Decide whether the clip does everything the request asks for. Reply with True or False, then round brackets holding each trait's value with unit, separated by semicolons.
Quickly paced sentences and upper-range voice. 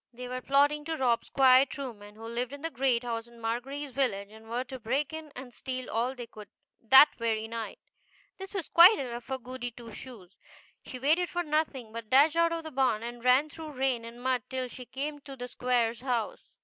True (215 wpm; 255 Hz)